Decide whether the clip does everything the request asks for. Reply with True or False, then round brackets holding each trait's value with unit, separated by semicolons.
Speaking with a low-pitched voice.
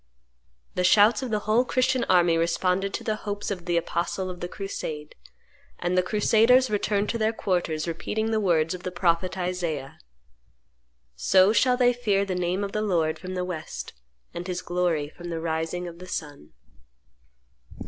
False (180 Hz)